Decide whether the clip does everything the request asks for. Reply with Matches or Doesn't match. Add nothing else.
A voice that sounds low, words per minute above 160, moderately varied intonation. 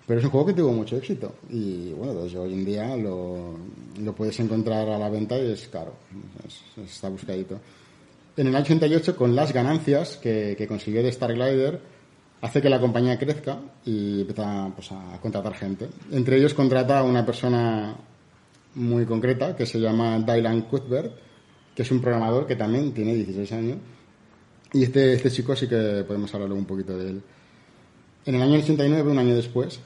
Matches